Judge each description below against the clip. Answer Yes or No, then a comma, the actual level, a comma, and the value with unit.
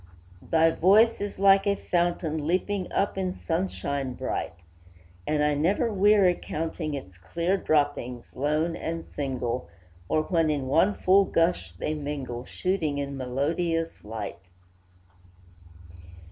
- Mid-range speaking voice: Yes, medium, 160 Hz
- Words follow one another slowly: Yes, slow, 125 wpm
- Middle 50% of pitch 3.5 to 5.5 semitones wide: Yes, average, 4.6 semitones